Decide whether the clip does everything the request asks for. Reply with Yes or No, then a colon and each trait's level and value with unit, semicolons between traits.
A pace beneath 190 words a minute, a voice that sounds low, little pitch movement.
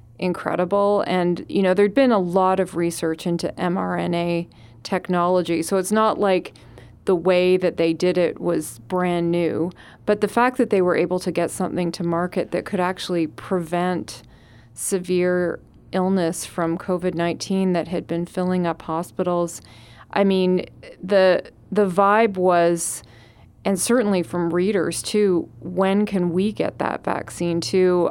No: average, 150 wpm; medium, 180 Hz; narrow, 1.9 semitones